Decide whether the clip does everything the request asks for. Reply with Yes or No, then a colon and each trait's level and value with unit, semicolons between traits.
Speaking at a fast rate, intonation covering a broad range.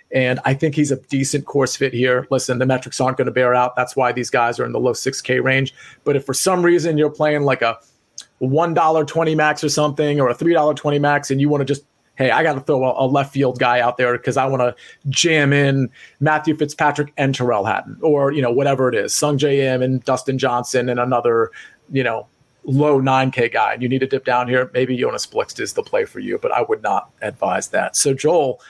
No: fast, 245 wpm; average, 2.7 semitones